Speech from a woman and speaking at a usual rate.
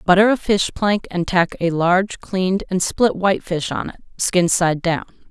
Yes: female; average, 190 wpm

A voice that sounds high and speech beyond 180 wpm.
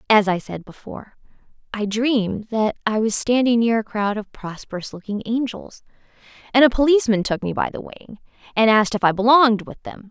Yes: high, 220 Hz; average, 190 wpm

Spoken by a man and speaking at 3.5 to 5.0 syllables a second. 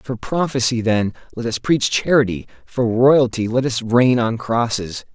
Yes: male; 4.3 syllables/s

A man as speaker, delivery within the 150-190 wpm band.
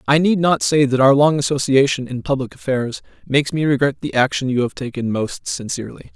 No: male; fast, 205 wpm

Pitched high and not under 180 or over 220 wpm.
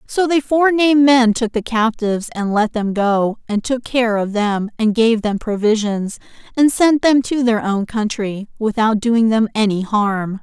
Yes: high, 225 Hz; average, 185 wpm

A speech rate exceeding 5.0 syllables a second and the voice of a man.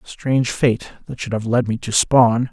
No: 4.4 syllables/s; male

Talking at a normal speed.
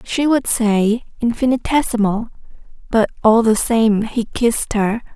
No: slow, 130 wpm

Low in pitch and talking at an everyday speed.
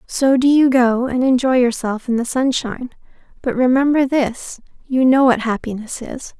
No: very high, 250 Hz; average, 160 wpm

